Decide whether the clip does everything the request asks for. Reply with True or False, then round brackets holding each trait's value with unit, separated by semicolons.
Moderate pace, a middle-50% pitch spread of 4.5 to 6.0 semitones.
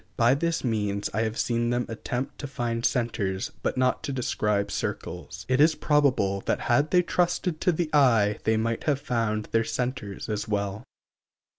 True (175 wpm; 4.8 semitones)